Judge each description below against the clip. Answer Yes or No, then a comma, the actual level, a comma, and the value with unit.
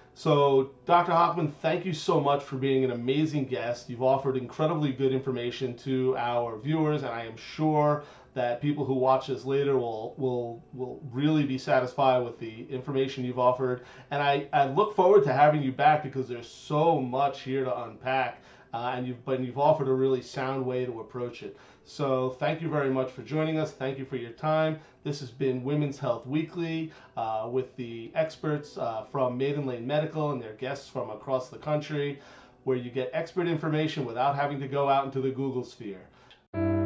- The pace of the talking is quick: No, average, 195 wpm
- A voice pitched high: No, low, 135 Hz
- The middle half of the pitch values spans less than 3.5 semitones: Yes, average, 2.7 semitones